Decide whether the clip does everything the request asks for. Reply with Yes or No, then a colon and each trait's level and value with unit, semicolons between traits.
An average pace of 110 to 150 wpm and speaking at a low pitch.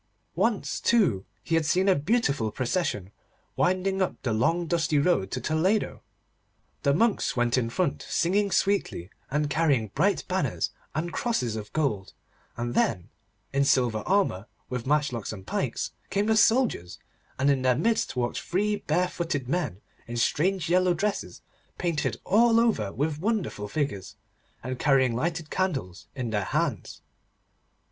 No: average, 145 wpm; medium, 150 Hz